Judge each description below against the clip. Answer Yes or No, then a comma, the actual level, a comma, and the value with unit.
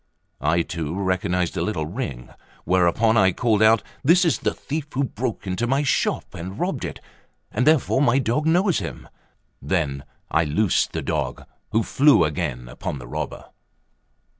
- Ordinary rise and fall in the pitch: No, wide, 8.0 semitones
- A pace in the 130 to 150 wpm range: No, average, 165 wpm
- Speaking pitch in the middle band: No, low, 105 Hz